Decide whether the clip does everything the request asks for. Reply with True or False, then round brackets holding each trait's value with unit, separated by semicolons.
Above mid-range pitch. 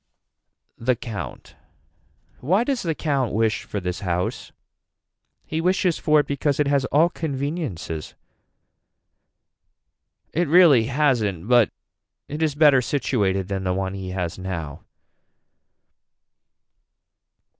False (130 Hz)